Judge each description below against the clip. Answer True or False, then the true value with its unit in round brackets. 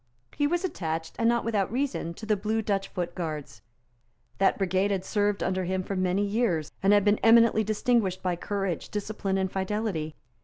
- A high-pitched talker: True (195 Hz)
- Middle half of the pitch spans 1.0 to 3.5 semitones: True (2.9 semitones)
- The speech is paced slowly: False (185 wpm)